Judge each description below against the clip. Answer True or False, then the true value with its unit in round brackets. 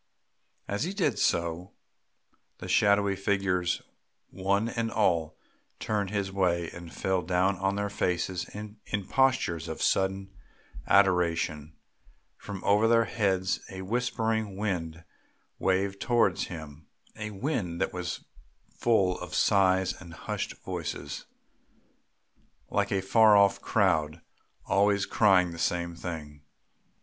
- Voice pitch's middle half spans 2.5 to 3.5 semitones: True (2.9 semitones)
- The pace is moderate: False (120 wpm)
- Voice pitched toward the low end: True (95 Hz)